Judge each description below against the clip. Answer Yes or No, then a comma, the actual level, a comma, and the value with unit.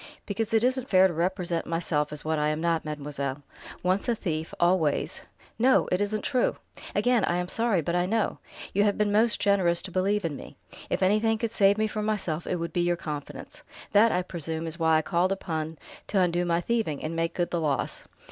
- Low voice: No, medium, 180 Hz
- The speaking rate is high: Yes, fast, 225 wpm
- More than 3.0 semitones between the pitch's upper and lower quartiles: Yes, average, 4.2 semitones